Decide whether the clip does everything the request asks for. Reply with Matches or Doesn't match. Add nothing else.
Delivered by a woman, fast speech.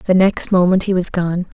Matches